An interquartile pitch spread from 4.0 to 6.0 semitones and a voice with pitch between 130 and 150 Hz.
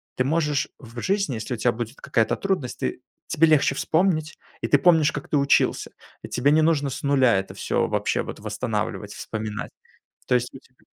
Yes: average, 4.3 semitones; medium, 140 Hz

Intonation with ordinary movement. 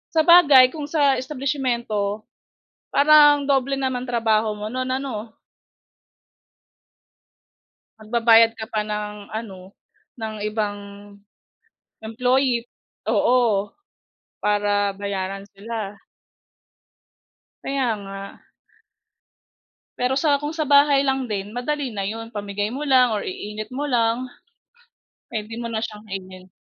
Yes: average, 4.3 semitones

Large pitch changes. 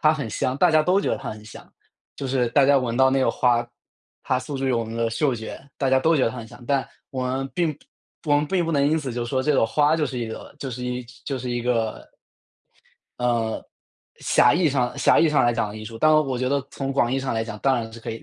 No: average, 3.2 semitones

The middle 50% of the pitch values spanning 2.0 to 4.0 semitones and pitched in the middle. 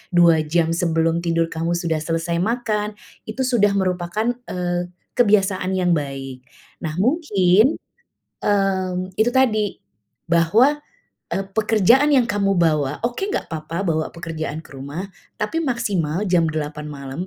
No: average, 4.5 semitones; medium, 180 Hz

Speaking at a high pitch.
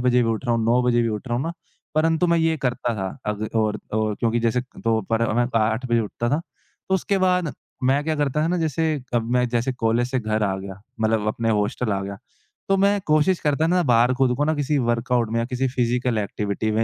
No: low, 120 Hz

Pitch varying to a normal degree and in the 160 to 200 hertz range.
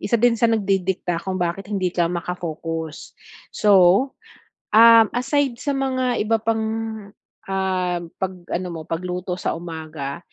Yes: average, 4.6 semitones; high, 190 Hz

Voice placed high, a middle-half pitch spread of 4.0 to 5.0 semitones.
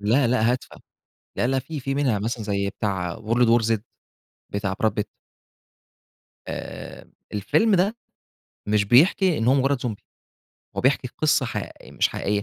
No: low, 120 Hz; average, 4.7 semitones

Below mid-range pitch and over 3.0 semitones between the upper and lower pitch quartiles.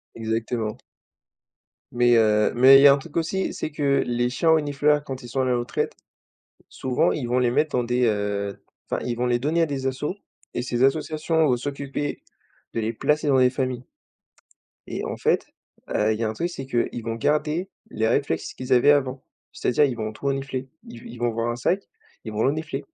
Yes: low, 130 Hz; average, 3.4 semitones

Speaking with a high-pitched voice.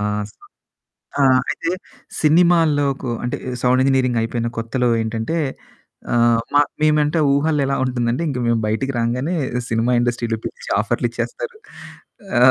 No: low, 130 Hz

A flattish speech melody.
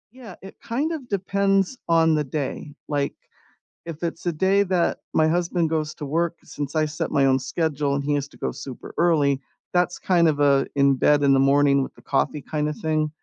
No: average, 3.6 semitones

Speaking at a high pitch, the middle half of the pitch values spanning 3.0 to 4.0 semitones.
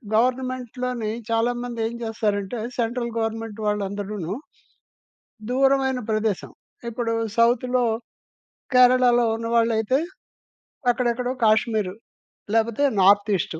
No: high, 230 Hz; narrow, 2.4 semitones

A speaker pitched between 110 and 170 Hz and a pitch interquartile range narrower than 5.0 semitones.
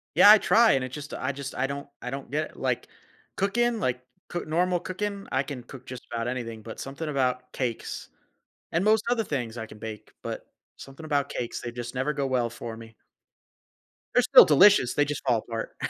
No: low, 135 Hz; wide, 5.6 semitones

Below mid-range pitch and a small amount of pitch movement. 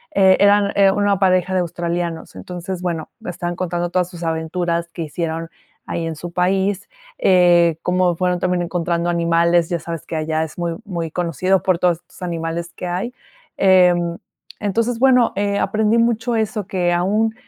No: medium, 175 Hz; narrow, 2.1 semitones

